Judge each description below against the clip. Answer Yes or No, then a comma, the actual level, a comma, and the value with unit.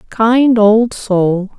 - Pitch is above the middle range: Yes, high, 215 Hz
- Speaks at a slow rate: Yes, slow, 115 wpm